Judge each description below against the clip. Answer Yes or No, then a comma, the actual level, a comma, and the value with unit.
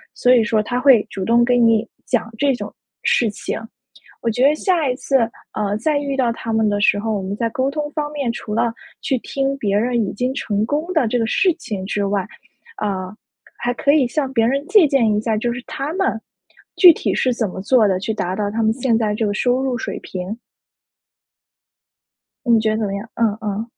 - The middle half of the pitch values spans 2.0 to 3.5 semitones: No, average, 4.1 semitones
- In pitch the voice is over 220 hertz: Yes, high, 230 Hz